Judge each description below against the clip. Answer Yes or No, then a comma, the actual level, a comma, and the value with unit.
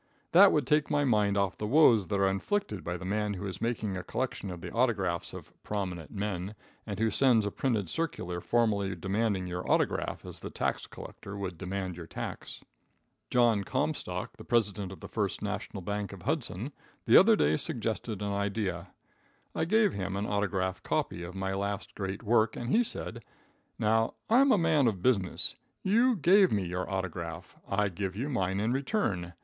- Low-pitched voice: Yes, low, 100 Hz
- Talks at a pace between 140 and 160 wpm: No, average, 185 wpm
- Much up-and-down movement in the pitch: No, average, 4.0 semitones